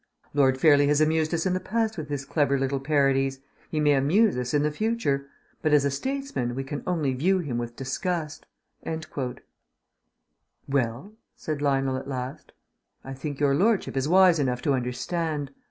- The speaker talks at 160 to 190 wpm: Yes, average, 170 wpm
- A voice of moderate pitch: Yes, medium, 145 Hz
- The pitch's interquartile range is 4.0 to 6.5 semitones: No, average, 3.5 semitones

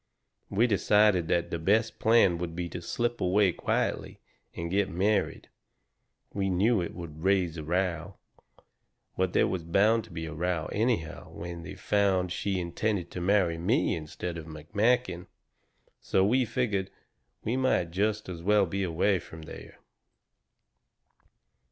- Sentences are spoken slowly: No, average, 145 wpm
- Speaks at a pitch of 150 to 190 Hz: No, very low, 95 Hz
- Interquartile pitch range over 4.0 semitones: No, average, 3.6 semitones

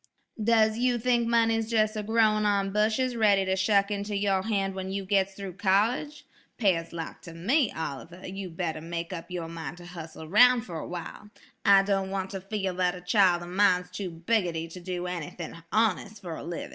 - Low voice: No, high, 195 Hz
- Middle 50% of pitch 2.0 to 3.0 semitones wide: No, average, 3.4 semitones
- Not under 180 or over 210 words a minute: Yes, average, 195 wpm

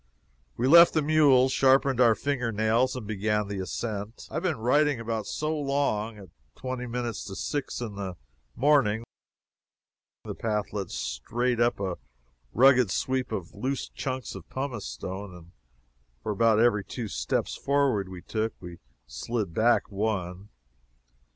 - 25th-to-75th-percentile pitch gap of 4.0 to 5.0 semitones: Yes, average, 4.5 semitones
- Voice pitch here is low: Yes, low, 115 Hz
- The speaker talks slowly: No, average, 150 wpm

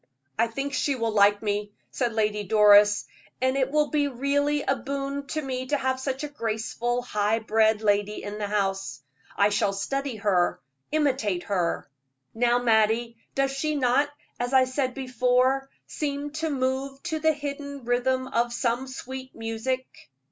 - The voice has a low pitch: No, very high, 255 Hz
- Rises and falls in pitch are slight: No, average, 4.0 semitones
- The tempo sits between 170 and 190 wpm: No, average, 160 wpm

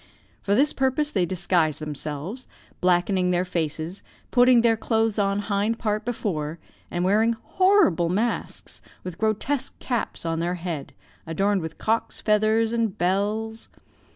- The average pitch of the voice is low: No, high, 205 Hz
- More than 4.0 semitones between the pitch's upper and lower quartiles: Yes, average, 4.4 semitones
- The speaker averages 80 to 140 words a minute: Yes, slow, 135 wpm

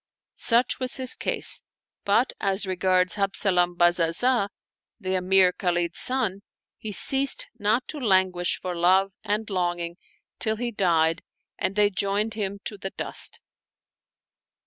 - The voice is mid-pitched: No, high, 195 Hz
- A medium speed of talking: No, slow, 130 wpm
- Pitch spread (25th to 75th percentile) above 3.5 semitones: No, average, 3.2 semitones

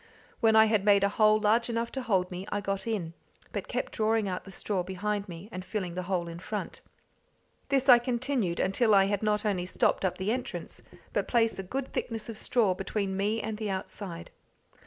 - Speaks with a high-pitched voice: Yes, high, 205 Hz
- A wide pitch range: No, average, 3.0 semitones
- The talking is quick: Yes, fast, 210 wpm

